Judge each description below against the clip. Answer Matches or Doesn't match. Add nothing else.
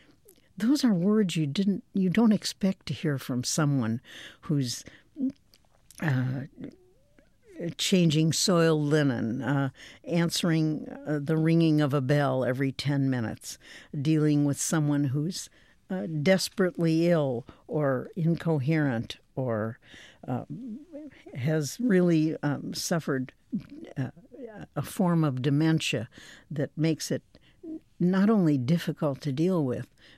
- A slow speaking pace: Matches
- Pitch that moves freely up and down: Doesn't match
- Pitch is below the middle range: Doesn't match